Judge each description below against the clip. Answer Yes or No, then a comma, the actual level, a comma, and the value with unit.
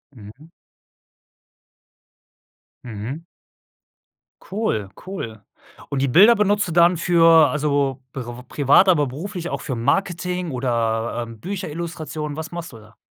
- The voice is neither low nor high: Yes, medium, 150 Hz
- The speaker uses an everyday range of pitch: No, wide, 6.0 semitones